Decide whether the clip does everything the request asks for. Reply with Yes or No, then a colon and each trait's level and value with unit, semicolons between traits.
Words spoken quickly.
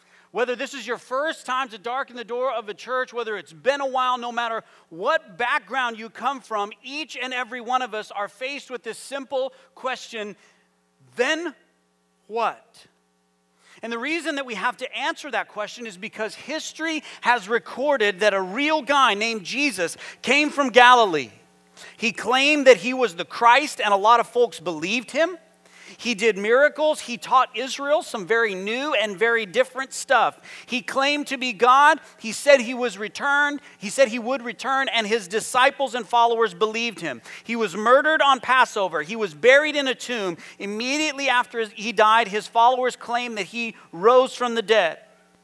No: average, 180 wpm